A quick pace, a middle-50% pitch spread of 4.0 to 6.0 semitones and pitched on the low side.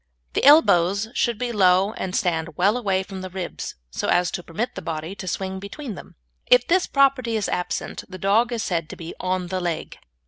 No: fast, 210 wpm; average, 4.3 semitones; high, 190 Hz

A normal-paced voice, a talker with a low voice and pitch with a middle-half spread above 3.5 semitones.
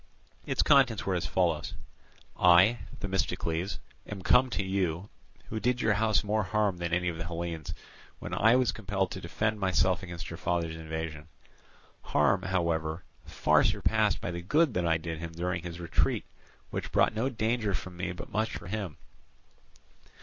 Yes: average, 165 wpm; very low, 90 Hz; average, 4.1 semitones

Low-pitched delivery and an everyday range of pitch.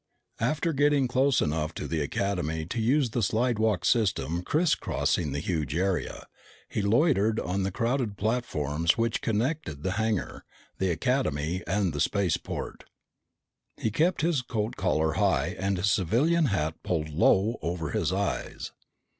No: low, 100 Hz; wide, 6.4 semitones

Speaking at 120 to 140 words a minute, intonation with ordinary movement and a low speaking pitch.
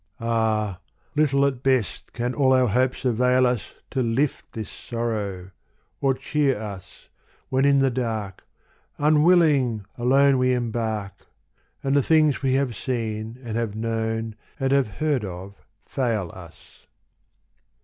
Yes: slow, 135 wpm; average, 3.6 semitones; low, 120 Hz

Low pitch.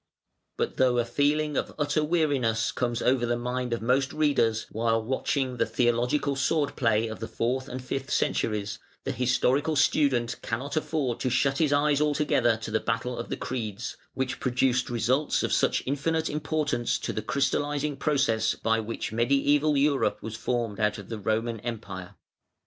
Yes: low, 125 Hz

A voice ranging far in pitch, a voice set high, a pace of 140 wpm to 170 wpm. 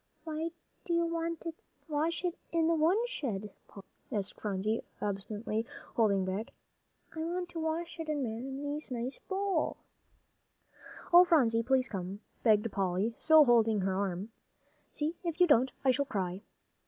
Yes: wide, 7.7 semitones; very high, 265 Hz; average, 150 wpm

